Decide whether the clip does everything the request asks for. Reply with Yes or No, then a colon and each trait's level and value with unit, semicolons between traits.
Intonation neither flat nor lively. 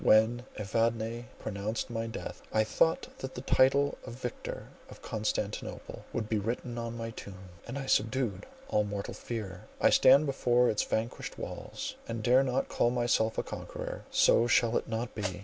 No: narrow, 2.2 semitones